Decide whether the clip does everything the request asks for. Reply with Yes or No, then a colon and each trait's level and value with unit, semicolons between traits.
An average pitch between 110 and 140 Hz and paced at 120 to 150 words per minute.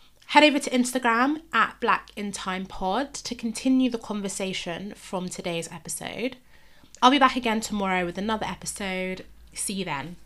No: high, 205 Hz; average, 140 wpm